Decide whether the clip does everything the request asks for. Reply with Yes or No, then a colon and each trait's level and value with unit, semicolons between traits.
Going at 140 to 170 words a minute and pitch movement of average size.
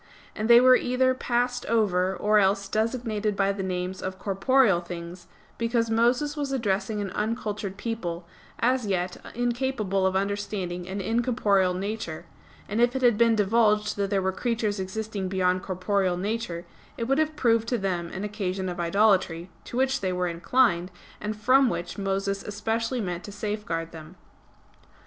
Yes: average, 165 wpm; average, 3.7 semitones